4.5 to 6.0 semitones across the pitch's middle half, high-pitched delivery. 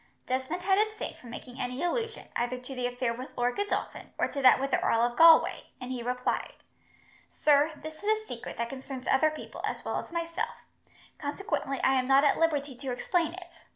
Yes: average, 5.0 semitones; very high, 275 Hz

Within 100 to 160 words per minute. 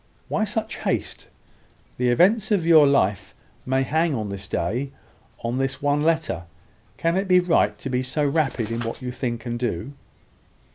No: average, 175 wpm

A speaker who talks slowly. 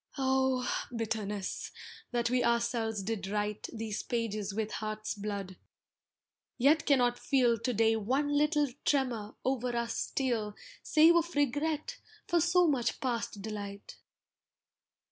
Yes: slow, 125 wpm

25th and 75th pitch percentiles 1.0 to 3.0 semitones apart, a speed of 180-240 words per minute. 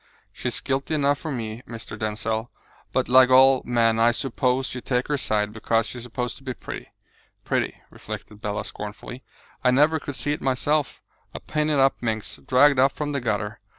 No: average, 3.4 semitones; average, 190 wpm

